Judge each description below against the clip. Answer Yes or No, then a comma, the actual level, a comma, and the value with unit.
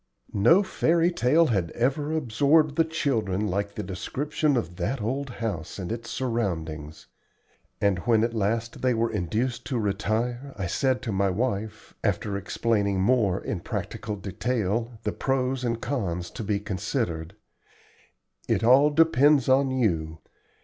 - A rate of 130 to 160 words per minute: Yes, average, 145 wpm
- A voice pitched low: Yes, low, 115 Hz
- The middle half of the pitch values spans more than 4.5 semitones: Yes, average, 4.9 semitones